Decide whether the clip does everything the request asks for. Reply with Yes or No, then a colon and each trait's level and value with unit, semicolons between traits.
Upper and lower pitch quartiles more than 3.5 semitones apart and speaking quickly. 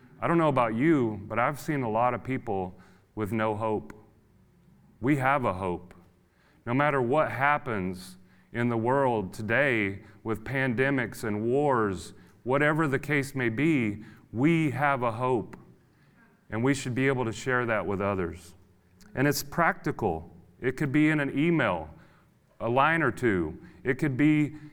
No: average, 5.3 semitones; average, 160 wpm